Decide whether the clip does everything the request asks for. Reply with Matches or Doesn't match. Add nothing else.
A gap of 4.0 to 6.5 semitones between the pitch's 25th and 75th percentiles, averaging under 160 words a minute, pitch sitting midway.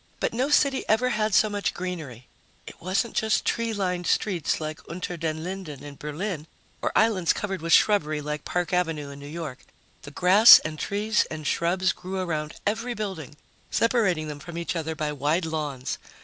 Doesn't match